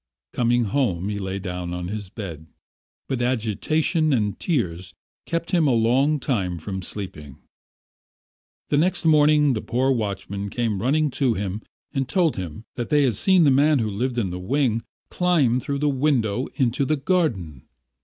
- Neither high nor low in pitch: No, low, 120 Hz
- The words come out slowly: No, average, 165 wpm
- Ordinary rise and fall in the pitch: No, wide, 6.6 semitones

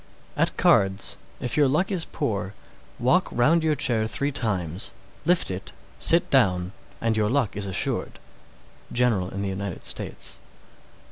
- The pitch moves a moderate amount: No, wide, 6.6 semitones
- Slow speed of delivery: No, average, 150 wpm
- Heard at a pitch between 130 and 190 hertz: No, low, 115 Hz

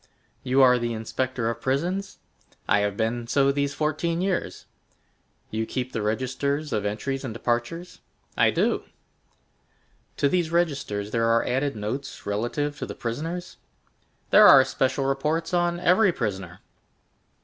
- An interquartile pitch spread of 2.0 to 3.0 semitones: No, average, 5.2 semitones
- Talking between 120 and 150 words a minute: Yes, average, 140 wpm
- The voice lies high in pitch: No, low, 135 Hz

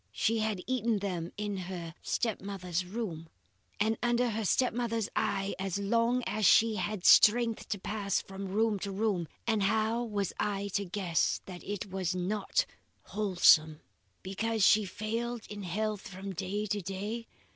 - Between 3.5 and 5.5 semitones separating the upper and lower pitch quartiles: No, average, 2.7 semitones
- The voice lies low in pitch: No, high, 205 Hz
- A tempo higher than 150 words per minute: Yes, average, 160 wpm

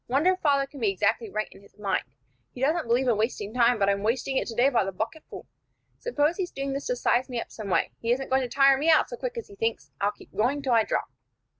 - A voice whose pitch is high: Yes, high, 245 Hz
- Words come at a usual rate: No, fast, 270 wpm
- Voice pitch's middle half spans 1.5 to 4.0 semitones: No, average, 4.6 semitones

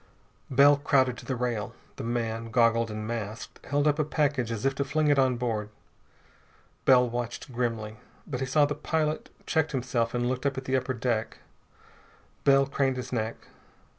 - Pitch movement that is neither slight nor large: Yes, average, 3.1 semitones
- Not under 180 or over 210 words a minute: Yes, average, 185 wpm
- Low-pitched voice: Yes, low, 125 Hz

